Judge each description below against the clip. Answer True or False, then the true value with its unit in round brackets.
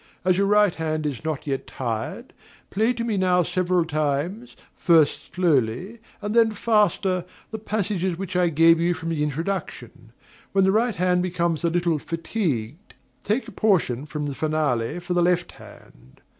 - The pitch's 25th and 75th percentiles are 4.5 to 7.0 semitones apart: False (4.1 semitones)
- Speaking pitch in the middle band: True (175 Hz)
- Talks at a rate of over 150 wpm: True (170 wpm)